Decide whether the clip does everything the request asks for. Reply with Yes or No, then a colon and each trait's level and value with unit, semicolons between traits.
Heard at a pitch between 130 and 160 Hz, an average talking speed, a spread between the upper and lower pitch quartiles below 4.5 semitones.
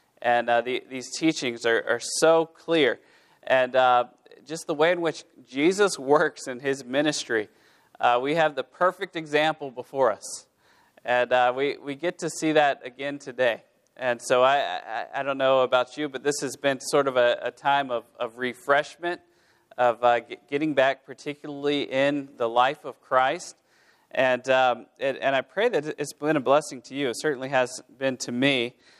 Yes: medium, 140 Hz; average, 185 wpm; average, 3.3 semitones